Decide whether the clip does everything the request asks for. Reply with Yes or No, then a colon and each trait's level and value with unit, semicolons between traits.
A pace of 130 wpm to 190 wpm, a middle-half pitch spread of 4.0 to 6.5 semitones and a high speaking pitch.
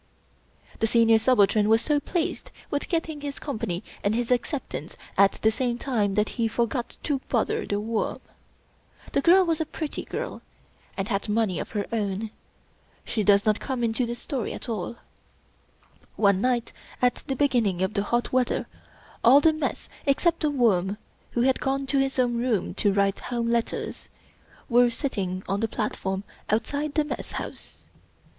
Yes: average, 170 wpm; average, 4.5 semitones; high, 235 Hz